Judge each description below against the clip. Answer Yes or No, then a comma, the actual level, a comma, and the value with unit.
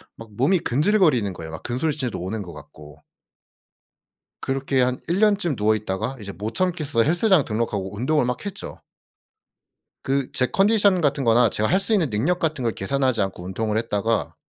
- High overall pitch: No, low, 125 Hz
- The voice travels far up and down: Yes, wide, 7.1 semitones